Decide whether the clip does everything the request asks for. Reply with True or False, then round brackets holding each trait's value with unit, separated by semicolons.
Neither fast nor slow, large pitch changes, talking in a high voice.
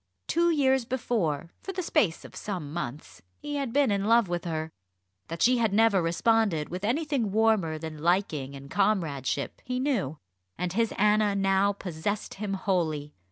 True (165 wpm; 6.0 semitones; 195 Hz)